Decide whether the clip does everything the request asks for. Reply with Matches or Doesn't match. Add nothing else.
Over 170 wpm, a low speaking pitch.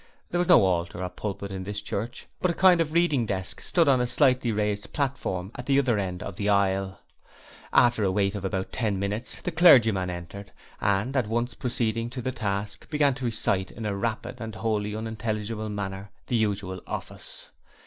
Matches